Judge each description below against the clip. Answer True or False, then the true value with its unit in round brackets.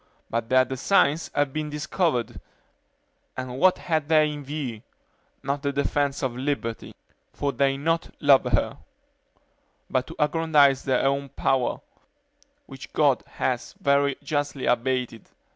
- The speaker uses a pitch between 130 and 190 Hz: True (140 Hz)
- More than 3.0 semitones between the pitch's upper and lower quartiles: False (2.4 semitones)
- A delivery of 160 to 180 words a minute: False (135 wpm)